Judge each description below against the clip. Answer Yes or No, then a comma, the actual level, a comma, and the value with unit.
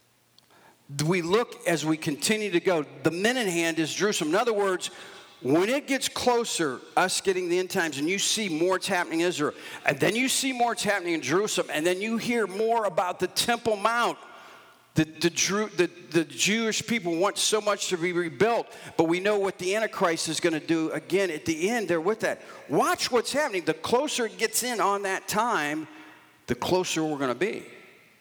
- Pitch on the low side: No, high, 190 Hz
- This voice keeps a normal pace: No, fast, 210 wpm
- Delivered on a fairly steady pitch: No, average, 5.1 semitones